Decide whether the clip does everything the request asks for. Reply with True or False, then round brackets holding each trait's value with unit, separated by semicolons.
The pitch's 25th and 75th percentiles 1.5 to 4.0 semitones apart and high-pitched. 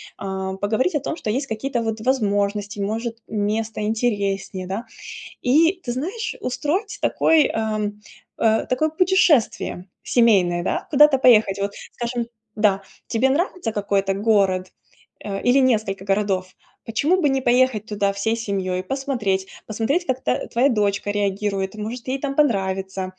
False (4.6 semitones; 220 Hz)